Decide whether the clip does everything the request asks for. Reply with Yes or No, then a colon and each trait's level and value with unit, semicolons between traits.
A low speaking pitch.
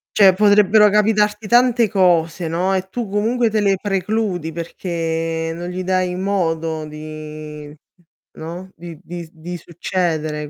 No: medium, 180 Hz